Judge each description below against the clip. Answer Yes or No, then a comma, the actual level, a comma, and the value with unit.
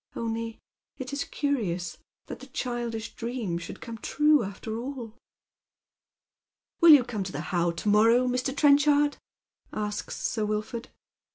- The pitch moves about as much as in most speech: Yes, average, 4.0 semitones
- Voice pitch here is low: No, high, 230 Hz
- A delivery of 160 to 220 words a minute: No, average, 145 wpm